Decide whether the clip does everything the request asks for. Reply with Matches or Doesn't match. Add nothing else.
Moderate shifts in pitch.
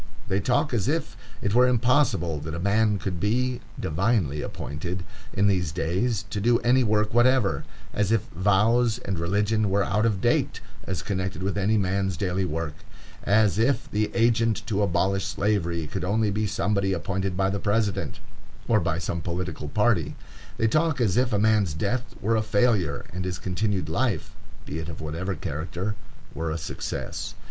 Matches